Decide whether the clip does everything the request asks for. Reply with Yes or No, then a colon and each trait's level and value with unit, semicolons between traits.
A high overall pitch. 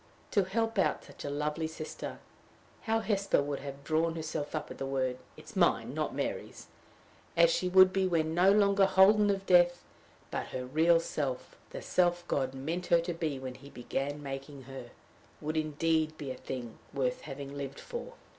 No: medium, 155 Hz